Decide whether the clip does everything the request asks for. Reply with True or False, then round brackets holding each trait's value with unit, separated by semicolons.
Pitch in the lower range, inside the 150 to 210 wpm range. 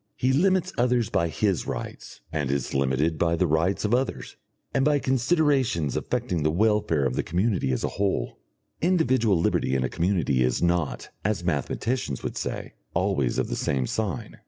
True (90 Hz; 175 wpm)